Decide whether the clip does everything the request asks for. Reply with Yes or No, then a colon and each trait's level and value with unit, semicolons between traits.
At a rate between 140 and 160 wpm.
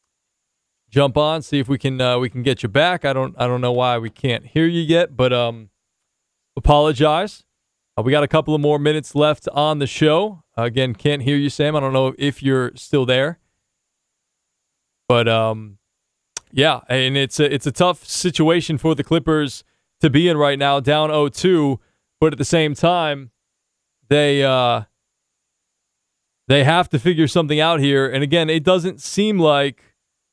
No: average, 180 wpm